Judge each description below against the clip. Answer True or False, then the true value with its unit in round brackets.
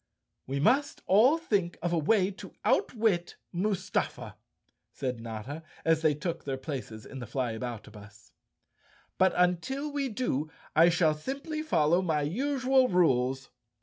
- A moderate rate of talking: True (145 wpm)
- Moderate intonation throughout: False (8.3 semitones)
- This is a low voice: False (170 Hz)